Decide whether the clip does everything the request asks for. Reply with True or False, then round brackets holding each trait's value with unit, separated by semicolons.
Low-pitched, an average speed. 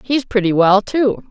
False (220 Hz; 185 wpm)